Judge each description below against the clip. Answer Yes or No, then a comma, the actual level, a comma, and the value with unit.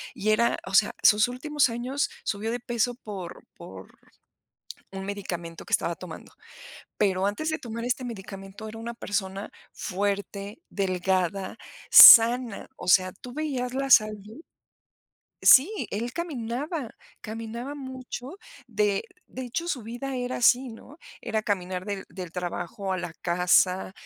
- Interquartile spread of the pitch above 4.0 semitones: Yes, average, 4.4 semitones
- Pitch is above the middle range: Yes, high, 220 Hz